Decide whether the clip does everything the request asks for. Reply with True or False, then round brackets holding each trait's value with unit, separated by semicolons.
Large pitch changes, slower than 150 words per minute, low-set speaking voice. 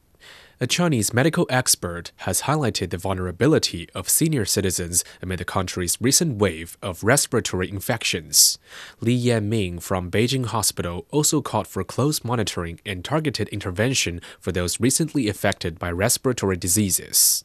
True (5.7 semitones; 135 wpm; 105 Hz)